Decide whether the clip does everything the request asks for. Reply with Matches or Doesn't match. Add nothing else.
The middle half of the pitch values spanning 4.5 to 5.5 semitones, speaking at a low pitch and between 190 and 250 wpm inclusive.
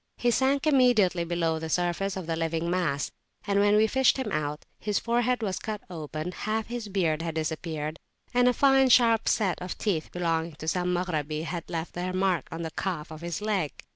Doesn't match